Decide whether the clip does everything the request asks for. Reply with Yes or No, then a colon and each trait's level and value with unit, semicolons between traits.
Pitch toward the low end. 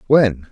Yes: low, 110 Hz